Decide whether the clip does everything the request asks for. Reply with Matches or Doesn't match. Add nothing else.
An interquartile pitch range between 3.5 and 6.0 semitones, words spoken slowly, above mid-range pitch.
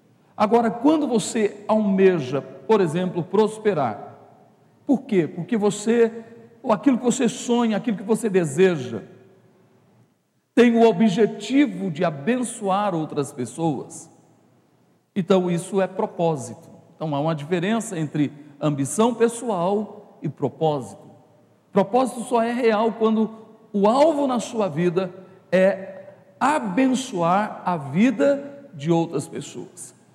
Matches